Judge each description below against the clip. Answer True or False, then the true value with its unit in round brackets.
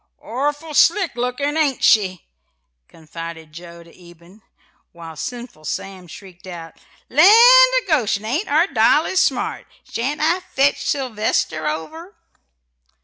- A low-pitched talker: False (240 Hz)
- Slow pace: True (120 wpm)